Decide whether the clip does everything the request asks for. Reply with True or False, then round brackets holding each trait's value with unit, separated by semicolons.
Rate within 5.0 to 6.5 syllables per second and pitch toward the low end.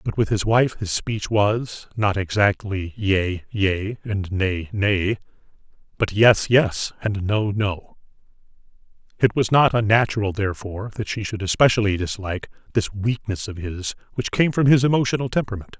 False (4.6 syllables/s; 105 Hz)